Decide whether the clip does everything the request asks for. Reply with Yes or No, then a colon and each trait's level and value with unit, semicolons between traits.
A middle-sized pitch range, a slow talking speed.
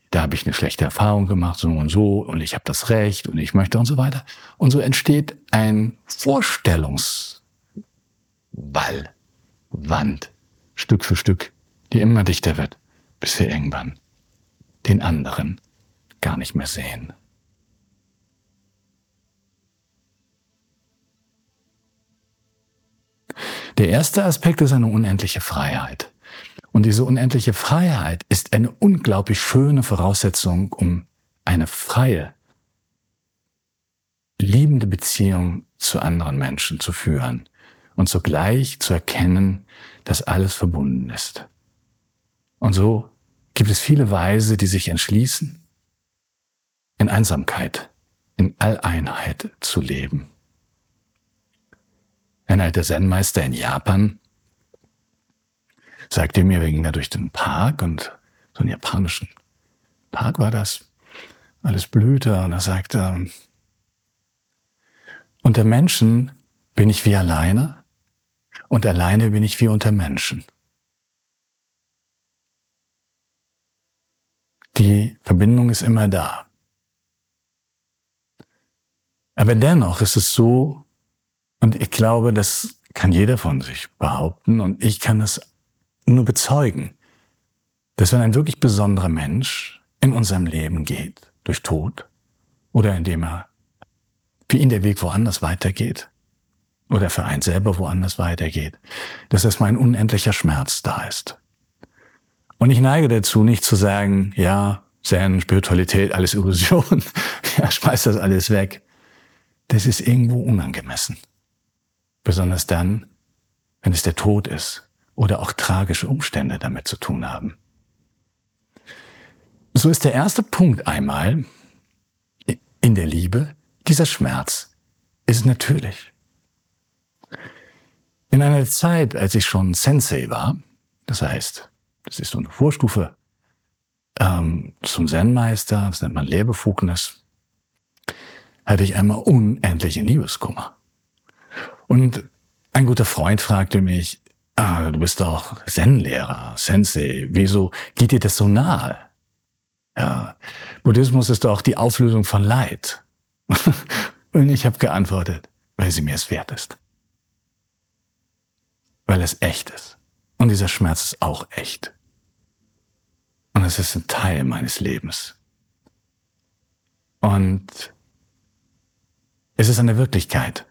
Yes: average, 4.5 semitones; slow, 115 wpm